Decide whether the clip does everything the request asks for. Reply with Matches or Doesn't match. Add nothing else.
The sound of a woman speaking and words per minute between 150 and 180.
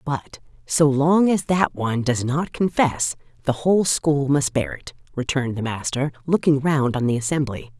Matches